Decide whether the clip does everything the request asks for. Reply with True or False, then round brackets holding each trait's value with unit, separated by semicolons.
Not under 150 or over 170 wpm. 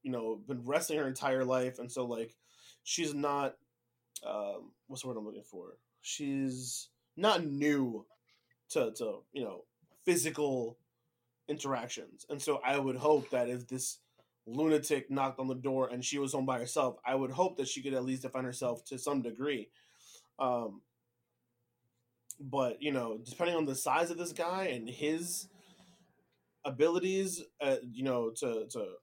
True (165 wpm)